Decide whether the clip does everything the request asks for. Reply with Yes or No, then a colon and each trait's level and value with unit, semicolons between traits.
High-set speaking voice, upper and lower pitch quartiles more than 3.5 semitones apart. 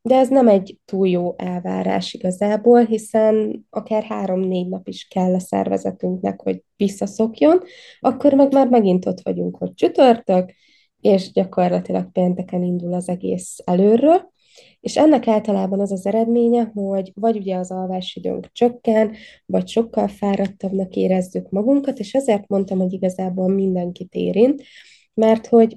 Yes: high, 195 Hz; average, 3.9 semitones